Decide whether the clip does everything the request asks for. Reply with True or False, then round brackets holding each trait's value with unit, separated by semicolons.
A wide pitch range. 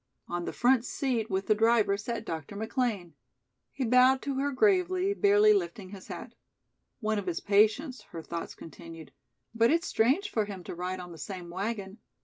True (5.9 semitones)